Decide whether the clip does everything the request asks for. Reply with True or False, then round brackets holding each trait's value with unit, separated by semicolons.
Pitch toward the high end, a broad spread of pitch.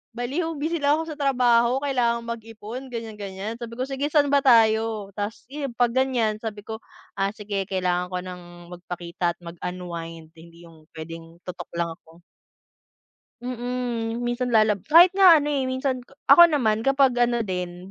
True (225 Hz; 6.1 semitones)